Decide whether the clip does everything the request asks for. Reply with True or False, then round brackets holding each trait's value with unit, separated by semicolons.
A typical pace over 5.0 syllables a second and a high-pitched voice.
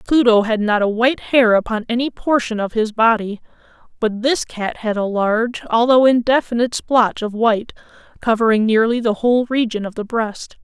True (5.3 syllables/s; 230 Hz)